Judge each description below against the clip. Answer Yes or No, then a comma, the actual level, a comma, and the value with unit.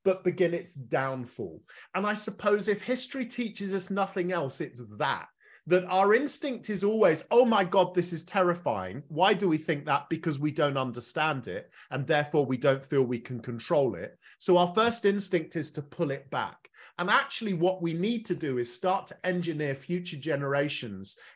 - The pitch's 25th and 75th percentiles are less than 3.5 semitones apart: No, wide, 5.5 semitones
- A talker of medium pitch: Yes, medium, 175 Hz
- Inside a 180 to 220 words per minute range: Yes, average, 190 wpm